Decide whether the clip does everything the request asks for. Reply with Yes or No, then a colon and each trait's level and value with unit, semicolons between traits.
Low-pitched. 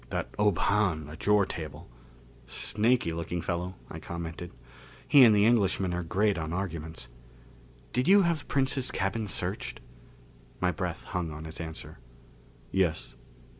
Yes: very low, 90 Hz